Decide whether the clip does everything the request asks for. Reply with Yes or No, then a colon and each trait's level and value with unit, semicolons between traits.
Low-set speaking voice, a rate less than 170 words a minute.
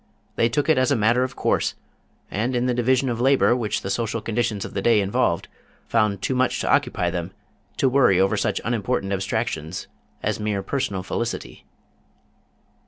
No: low, 115 Hz; average, 175 wpm